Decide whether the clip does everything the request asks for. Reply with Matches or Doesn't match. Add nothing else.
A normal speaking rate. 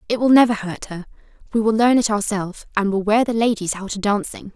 Doesn't match